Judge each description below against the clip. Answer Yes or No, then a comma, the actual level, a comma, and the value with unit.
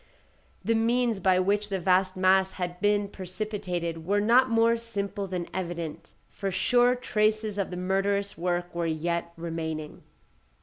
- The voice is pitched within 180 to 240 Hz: Yes, high, 190 Hz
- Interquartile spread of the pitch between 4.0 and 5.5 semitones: No, average, 3.2 semitones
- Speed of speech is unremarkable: Yes, average, 145 wpm